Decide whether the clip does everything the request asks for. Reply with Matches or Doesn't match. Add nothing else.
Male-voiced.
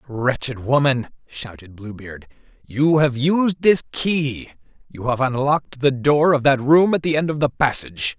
Matches